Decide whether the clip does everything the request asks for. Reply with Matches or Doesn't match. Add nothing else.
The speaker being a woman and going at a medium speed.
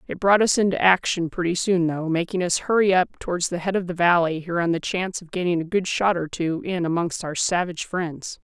Doesn't match